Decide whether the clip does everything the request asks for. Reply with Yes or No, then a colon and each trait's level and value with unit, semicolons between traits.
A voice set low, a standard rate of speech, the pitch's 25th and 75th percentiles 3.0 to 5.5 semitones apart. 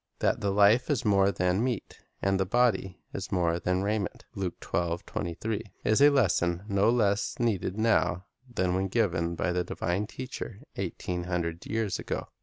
Yes: low, 100 Hz; average, 160 wpm; average, 3.6 semitones